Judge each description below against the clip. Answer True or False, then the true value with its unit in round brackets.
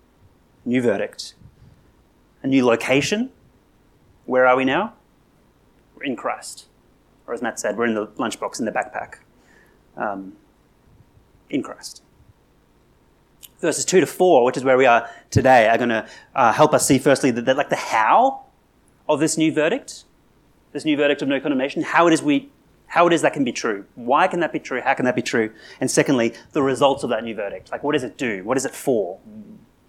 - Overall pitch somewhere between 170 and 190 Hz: False (140 Hz)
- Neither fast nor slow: True (195 wpm)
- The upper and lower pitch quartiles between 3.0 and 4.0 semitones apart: False (4.6 semitones)